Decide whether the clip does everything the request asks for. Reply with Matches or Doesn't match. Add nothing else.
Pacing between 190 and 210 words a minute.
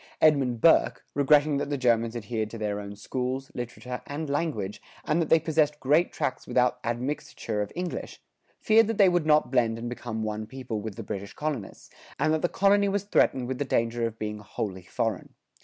Matches